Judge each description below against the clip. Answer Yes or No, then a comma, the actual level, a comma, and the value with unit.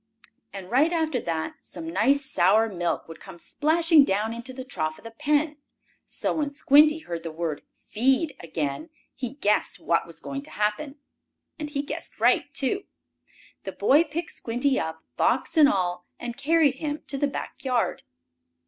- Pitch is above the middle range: Yes, very high, 255 Hz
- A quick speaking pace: No, average, 170 wpm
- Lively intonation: Yes, wide, 8.6 semitones